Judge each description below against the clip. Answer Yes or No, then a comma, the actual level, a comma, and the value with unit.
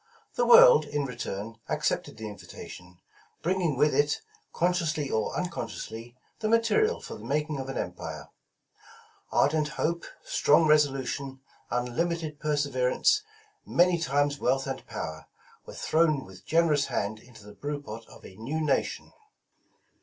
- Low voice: No, medium, 145 Hz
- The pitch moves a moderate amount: Yes, average, 5.0 semitones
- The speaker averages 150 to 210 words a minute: No, average, 140 wpm